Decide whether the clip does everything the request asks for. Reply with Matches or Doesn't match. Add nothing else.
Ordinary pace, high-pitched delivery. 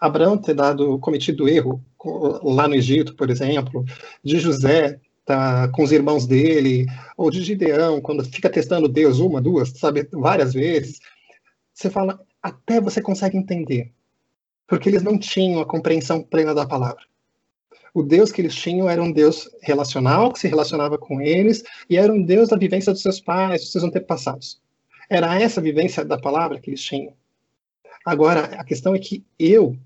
Doesn't match